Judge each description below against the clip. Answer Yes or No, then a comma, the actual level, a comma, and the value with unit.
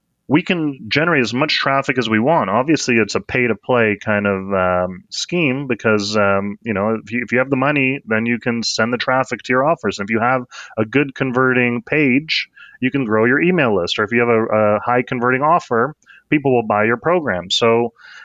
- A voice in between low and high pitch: No, low, 120 Hz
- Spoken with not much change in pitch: No, average, 3.4 semitones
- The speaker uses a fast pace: Yes, fast, 225 wpm